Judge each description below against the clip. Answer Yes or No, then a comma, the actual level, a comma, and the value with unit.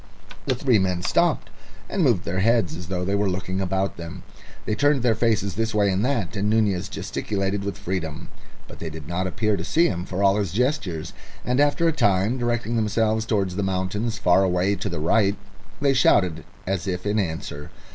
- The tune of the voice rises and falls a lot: No, average, 3.6 semitones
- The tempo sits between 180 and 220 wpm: Yes, average, 200 wpm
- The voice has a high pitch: No, low, 100 Hz